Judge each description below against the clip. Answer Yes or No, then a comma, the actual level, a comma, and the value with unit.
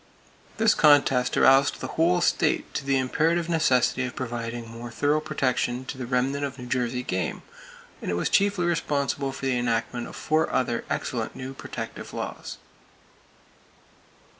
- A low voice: Yes, low, 130 Hz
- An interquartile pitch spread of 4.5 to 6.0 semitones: No, average, 3.5 semitones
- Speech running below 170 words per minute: Yes, average, 155 wpm